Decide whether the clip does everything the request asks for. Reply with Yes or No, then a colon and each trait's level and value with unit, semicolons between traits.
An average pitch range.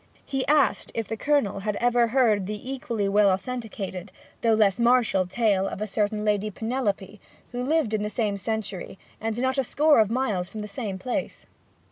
Yes: average, 3.6 semitones